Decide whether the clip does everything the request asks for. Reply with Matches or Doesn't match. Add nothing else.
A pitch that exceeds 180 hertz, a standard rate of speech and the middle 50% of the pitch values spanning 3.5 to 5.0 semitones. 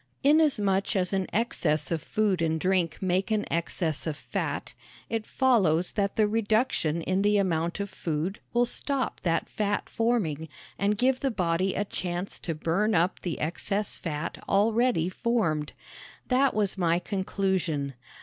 Matches